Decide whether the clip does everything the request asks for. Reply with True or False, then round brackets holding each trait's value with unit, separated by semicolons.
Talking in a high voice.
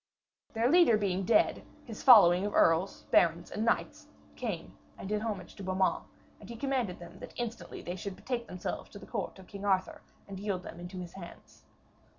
True (195 Hz)